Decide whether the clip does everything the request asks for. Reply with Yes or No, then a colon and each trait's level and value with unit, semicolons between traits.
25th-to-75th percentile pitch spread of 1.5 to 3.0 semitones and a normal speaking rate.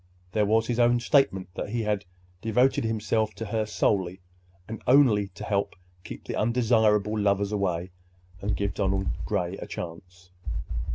Yes: narrow, 2.5 semitones; average, 155 wpm